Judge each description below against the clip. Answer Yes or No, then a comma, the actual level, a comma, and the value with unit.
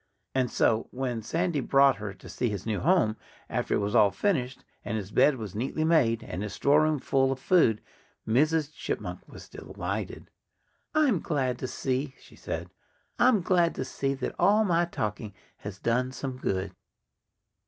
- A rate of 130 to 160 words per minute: No, average, 175 wpm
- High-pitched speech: No, low, 130 Hz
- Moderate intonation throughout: No, wide, 6.1 semitones